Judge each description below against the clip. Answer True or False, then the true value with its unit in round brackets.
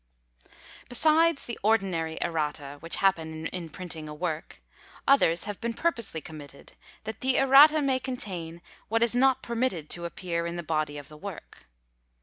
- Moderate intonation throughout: False (7.3 semitones)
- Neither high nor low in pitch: True (180 Hz)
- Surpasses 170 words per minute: False (155 wpm)